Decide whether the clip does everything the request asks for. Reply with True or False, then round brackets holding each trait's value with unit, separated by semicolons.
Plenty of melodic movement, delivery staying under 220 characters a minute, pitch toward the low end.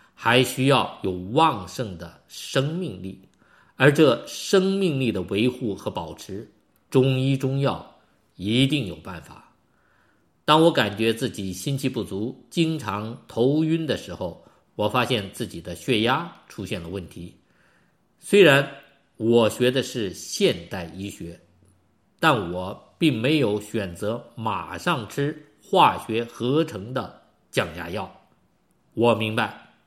True (5.7 semitones; 185 characters per minute; 115 Hz)